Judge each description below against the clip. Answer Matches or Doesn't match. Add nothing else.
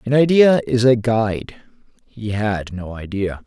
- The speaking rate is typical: Matches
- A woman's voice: Doesn't match